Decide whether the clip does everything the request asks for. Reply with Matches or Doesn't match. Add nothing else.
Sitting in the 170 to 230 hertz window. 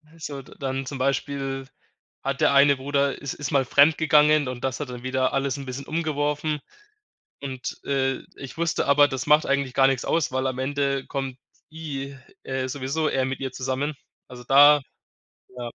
Doesn't match